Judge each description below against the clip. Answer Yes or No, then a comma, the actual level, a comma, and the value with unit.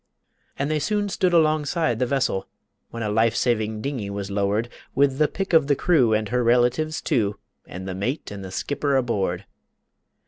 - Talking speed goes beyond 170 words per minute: Yes, average, 180 wpm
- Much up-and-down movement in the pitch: Yes, wide, 6.0 semitones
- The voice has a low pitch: Yes, low, 120 Hz